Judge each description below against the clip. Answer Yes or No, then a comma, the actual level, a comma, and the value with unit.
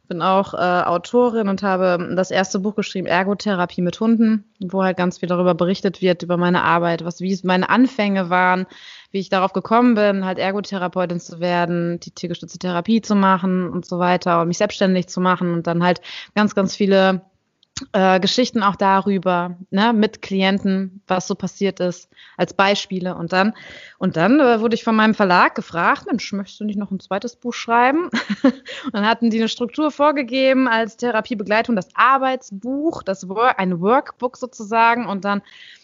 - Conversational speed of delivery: Yes, average, 180 wpm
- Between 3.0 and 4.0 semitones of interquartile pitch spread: Yes, average, 3.6 semitones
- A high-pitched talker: Yes, high, 195 Hz